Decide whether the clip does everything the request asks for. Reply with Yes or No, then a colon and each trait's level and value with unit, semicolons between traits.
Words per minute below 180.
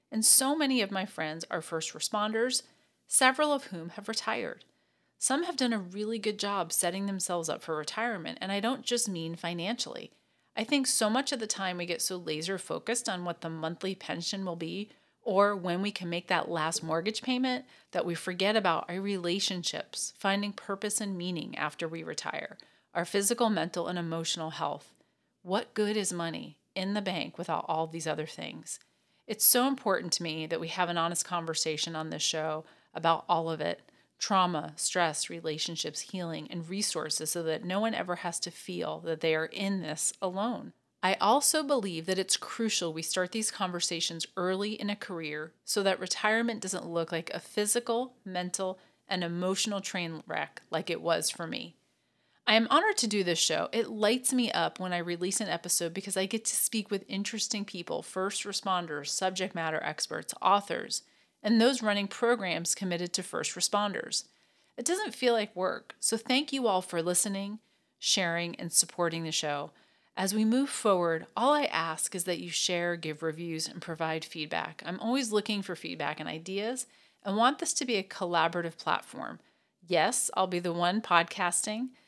No: average, 185 wpm